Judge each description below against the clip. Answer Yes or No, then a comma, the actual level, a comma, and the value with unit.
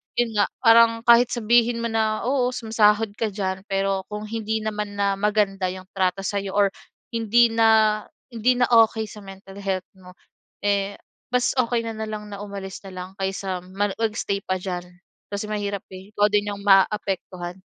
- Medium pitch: No, high, 205 Hz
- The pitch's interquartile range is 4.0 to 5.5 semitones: No, narrow, 2.5 semitones